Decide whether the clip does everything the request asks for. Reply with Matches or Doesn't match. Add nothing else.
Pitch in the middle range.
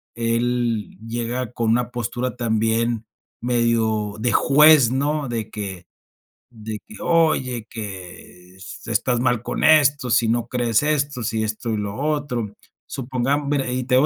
Doesn't match